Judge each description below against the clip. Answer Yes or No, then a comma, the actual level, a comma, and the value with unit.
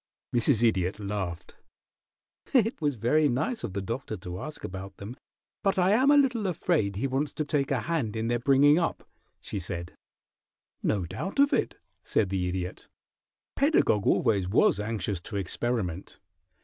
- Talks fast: No, average, 160 wpm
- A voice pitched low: Yes, low, 115 Hz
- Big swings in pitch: Yes, wide, 8.0 semitones